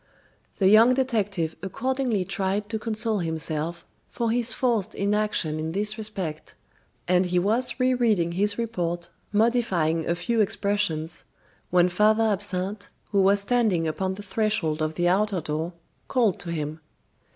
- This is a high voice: Yes, high, 200 Hz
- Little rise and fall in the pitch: No, average, 4.2 semitones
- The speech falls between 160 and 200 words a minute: No, average, 140 wpm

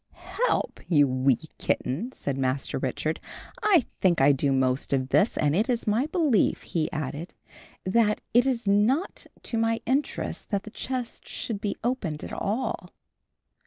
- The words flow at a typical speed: Yes, average, 160 wpm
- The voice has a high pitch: Yes, high, 205 Hz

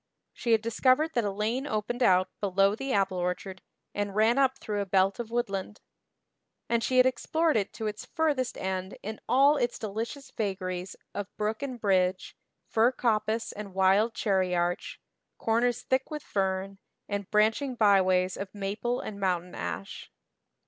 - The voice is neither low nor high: No, high, 210 Hz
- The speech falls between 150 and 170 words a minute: Yes, average, 160 wpm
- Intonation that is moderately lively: Yes, average, 3.9 semitones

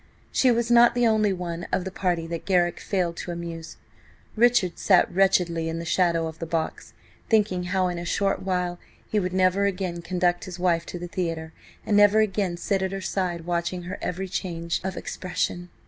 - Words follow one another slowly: No, average, 195 wpm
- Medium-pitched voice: Yes, medium, 180 Hz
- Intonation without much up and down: Yes, narrow, 2.1 semitones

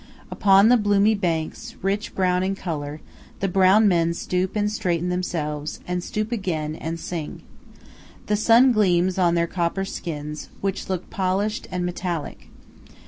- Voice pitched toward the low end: No, medium, 185 Hz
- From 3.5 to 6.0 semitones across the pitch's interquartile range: No, average, 3.0 semitones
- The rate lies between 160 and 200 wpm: No, average, 145 wpm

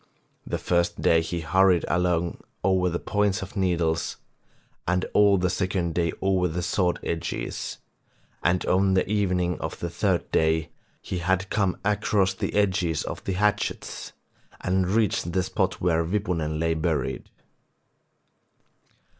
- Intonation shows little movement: Yes, narrow, 2.1 semitones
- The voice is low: Yes, very low, 90 Hz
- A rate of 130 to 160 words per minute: Yes, average, 140 wpm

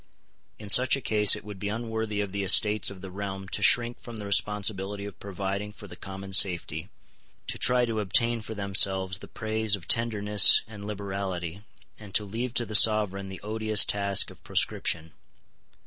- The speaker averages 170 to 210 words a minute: Yes, average, 180 wpm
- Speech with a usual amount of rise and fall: No, narrow, 2.0 semitones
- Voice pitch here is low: Yes, low, 100 Hz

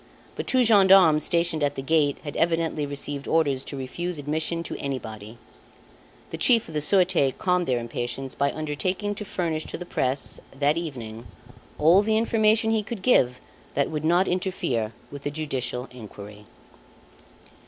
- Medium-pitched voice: Yes, medium, 155 Hz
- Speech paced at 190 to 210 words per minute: No, average, 160 wpm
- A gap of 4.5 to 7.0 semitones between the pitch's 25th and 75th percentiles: Yes, average, 5.2 semitones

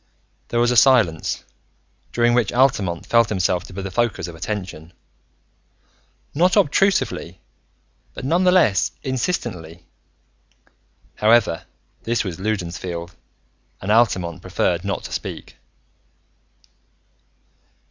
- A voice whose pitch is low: Yes, low, 105 Hz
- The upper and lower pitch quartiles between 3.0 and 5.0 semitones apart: No, wide, 5.4 semitones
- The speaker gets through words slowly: Yes, slow, 105 wpm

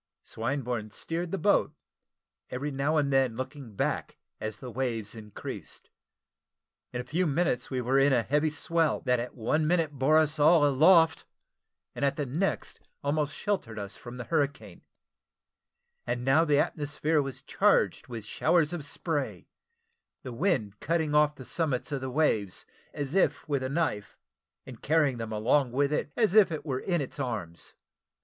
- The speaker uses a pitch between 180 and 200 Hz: No, medium, 140 Hz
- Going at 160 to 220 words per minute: Yes, average, 165 wpm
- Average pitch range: Yes, average, 4.1 semitones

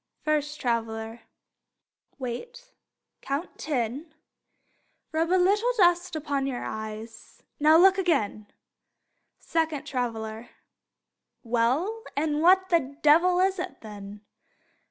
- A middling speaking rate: No, slow, 100 wpm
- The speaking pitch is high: Yes, very high, 295 Hz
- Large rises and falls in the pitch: Yes, wide, 7.2 semitones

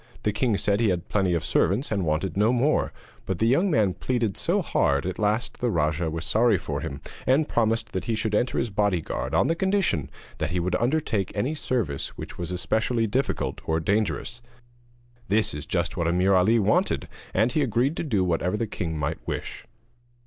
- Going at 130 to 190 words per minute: No, average, 200 wpm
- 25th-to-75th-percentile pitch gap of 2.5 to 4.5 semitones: No, average, 5.1 semitones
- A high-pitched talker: No, low, 105 Hz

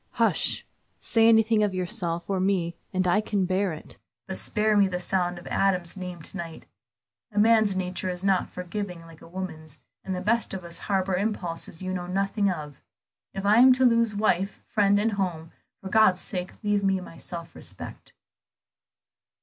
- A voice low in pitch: No, high, 190 Hz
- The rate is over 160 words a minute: Yes, average, 180 wpm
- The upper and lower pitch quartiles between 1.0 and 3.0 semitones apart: Yes, average, 2.7 semitones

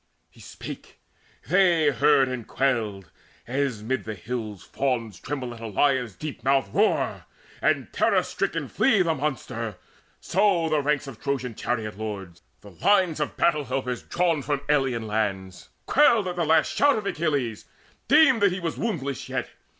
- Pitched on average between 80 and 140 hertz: Yes, low, 135 Hz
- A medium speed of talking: Yes, average, 160 wpm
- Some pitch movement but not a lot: No, wide, 6.4 semitones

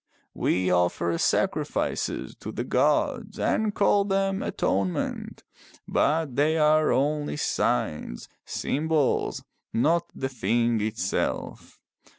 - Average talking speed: No, slow, 100 wpm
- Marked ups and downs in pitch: Yes, wide, 8.1 semitones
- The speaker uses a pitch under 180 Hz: Yes, medium, 140 Hz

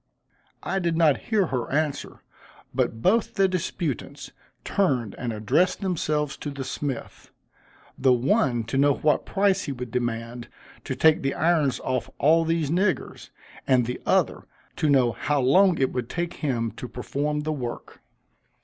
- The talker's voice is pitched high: No, medium, 145 Hz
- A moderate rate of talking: Yes, average, 160 wpm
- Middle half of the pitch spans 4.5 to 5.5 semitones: Yes, average, 5.2 semitones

